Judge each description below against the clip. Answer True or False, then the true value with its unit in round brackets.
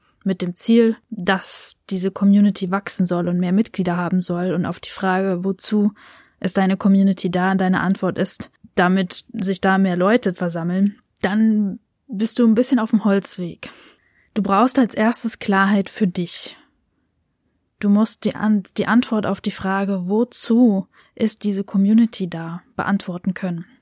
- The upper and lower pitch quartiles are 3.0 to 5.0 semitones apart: False (2.5 semitones)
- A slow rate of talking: False (160 wpm)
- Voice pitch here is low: False (195 Hz)